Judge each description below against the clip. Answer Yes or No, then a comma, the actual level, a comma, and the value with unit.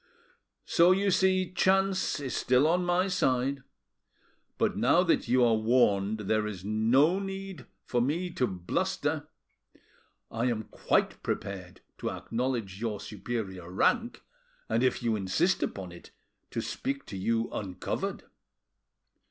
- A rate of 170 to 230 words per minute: No, slow, 135 wpm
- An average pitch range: No, wide, 8.8 semitones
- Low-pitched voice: Yes, low, 125 Hz